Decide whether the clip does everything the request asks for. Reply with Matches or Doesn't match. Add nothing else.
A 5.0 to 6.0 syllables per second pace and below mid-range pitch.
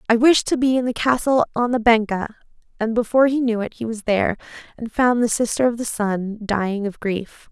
Doesn't match